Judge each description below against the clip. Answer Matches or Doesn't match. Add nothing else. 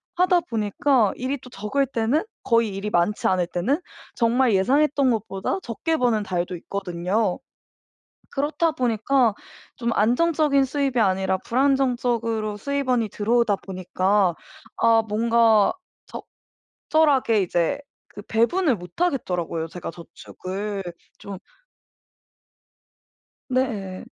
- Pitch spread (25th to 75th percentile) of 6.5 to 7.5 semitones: Doesn't match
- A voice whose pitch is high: Matches